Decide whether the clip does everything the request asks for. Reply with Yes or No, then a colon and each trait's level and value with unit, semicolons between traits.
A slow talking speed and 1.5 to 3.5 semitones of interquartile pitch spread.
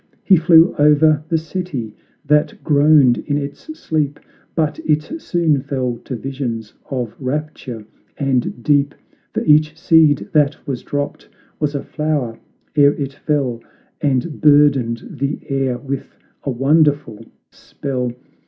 Yes: slow, 130 wpm; narrow, 2.6 semitones